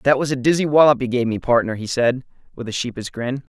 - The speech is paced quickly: Yes, fast, 255 wpm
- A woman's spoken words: No, male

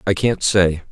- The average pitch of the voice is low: Yes, very low, 95 Hz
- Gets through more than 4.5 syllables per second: No, 4.1 syllables/s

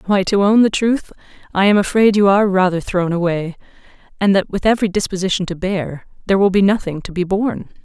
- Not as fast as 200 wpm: No, fast, 205 wpm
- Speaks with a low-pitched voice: No, high, 195 Hz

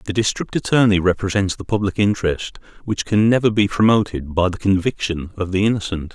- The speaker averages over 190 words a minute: No, average, 175 wpm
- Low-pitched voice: Yes, low, 100 Hz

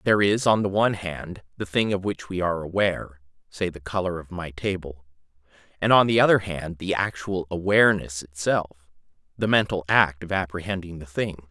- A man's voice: Yes, male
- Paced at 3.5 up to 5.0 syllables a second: No, 5.5 syllables/s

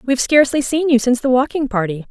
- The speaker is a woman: Yes, female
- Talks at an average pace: No, fast, 255 wpm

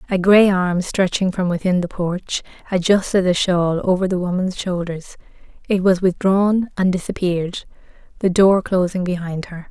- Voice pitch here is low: No, medium, 185 Hz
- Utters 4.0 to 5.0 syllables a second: Yes, 4.7 syllables/s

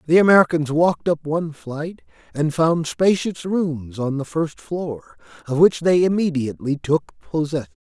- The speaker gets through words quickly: No, average, 155 wpm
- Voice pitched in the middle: Yes, medium, 155 Hz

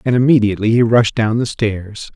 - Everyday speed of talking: Yes, average, 195 wpm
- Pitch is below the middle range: Yes, low, 115 Hz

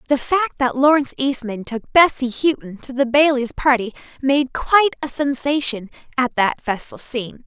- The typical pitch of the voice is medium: No, very high, 265 Hz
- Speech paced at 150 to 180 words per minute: Yes, average, 160 wpm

